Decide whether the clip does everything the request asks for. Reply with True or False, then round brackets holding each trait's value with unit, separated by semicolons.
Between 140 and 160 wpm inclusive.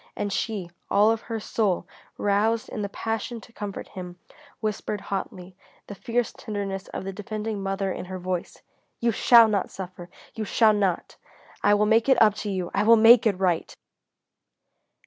False (175 wpm)